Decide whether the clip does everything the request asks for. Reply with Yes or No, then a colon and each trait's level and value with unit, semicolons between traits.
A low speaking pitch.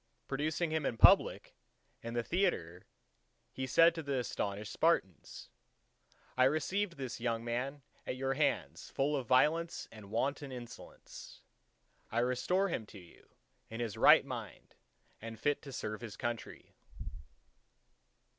Yes: low, 130 Hz